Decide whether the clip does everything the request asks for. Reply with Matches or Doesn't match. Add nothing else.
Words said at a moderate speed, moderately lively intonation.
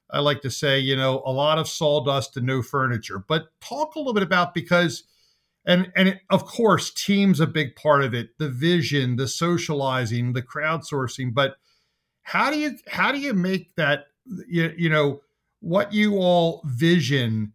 Matches